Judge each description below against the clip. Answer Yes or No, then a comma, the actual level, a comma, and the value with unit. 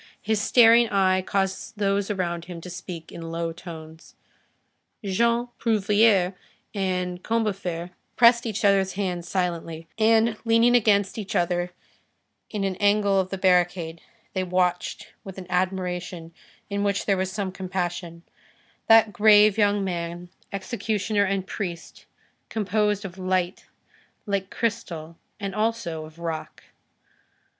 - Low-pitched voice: No, high, 190 Hz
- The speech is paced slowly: Yes, slow, 130 wpm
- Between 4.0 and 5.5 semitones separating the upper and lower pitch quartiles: No, average, 2.9 semitones